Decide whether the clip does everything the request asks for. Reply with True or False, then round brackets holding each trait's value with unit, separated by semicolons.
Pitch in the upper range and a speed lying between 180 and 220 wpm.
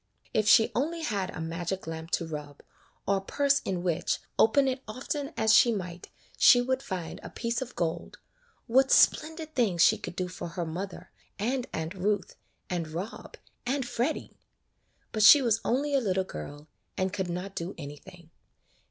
True (195 Hz; 185 wpm)